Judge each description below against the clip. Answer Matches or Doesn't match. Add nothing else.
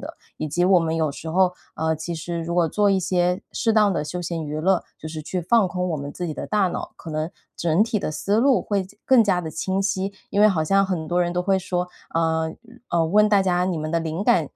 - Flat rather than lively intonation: Doesn't match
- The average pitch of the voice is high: Doesn't match